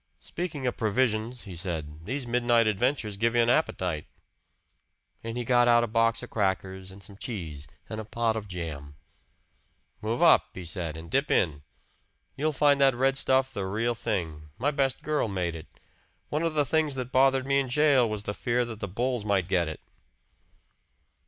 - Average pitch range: No, wide, 5.7 semitones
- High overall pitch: No, low, 115 Hz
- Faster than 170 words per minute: Yes, average, 185 wpm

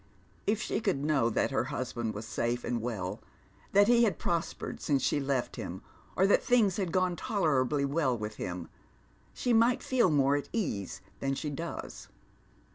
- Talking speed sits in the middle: Yes, average, 175 wpm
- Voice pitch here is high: No, medium, 145 Hz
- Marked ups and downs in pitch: Yes, wide, 8.0 semitones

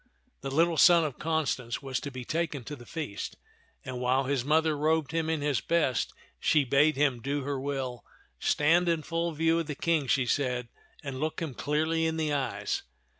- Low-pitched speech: No, medium, 145 Hz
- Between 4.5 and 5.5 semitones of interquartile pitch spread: No, average, 3.3 semitones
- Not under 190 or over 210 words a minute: Yes, fast, 205 wpm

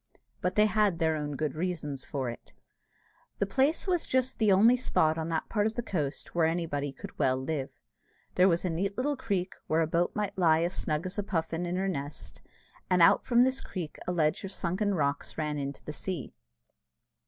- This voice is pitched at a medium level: Yes, medium, 175 Hz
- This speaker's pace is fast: Yes, fast, 210 wpm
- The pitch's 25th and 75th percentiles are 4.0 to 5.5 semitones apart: Yes, average, 4.7 semitones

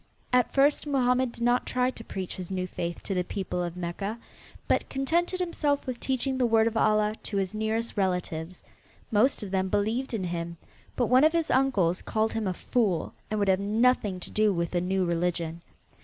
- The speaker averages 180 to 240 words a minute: Yes, average, 200 wpm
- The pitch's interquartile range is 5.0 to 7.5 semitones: Yes, wide, 5.5 semitones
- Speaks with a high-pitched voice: Yes, high, 215 Hz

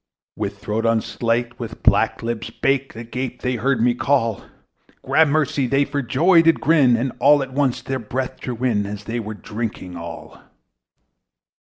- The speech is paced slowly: No, average, 160 wpm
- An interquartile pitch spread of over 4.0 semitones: No, average, 3.3 semitones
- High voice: No, low, 125 Hz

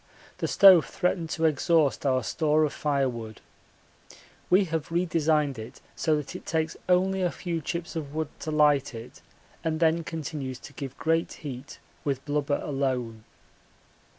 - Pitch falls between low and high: Yes, medium, 155 Hz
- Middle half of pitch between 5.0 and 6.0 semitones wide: No, average, 3.1 semitones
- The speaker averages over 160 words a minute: No, average, 150 wpm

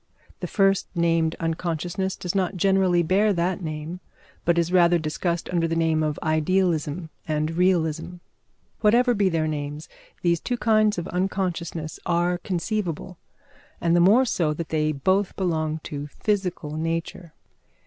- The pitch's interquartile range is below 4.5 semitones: Yes, average, 2.8 semitones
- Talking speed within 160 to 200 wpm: No, average, 145 wpm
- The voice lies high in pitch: No, medium, 170 Hz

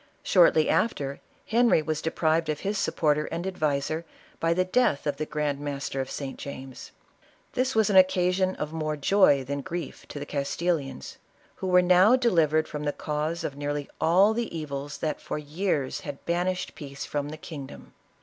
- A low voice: No, medium, 155 Hz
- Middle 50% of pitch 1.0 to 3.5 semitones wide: No, average, 4.0 semitones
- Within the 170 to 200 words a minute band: Yes, average, 175 wpm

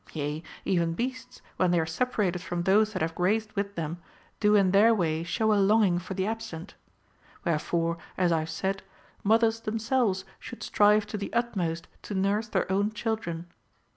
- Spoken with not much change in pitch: No, average, 4.2 semitones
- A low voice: No, high, 195 Hz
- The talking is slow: No, average, 175 wpm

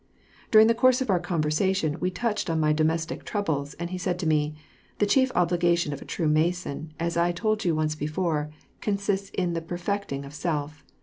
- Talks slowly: No, average, 195 wpm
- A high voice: No, medium, 170 Hz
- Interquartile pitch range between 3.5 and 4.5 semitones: Yes, average, 3.9 semitones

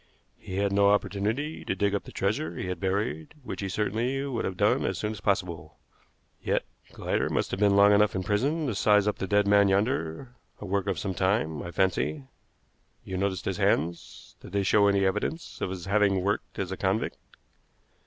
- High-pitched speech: No, low, 100 Hz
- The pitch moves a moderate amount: No, narrow, 1.8 semitones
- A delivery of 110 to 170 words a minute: No, fast, 205 wpm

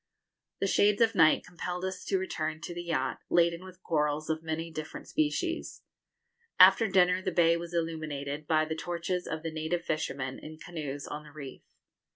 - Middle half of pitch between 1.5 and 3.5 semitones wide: Yes, narrow, 2.5 semitones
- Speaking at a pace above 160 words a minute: Yes, average, 180 wpm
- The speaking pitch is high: No, medium, 165 Hz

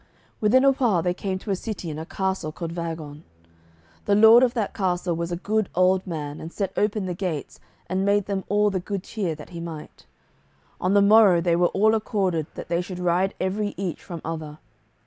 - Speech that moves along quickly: Yes, fast, 210 wpm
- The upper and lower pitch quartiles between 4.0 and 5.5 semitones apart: No, average, 3.3 semitones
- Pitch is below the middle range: No, medium, 185 Hz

